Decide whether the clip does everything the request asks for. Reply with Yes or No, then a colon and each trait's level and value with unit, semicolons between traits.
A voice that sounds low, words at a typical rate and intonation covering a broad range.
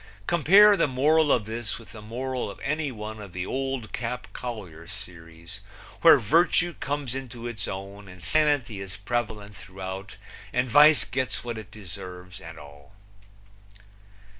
Yes: low, 110 Hz; average, 150 wpm; wide, 5.7 semitones